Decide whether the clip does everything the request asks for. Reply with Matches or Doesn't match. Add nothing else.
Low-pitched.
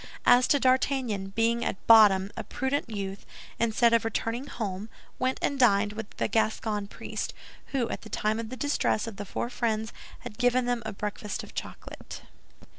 Doesn't match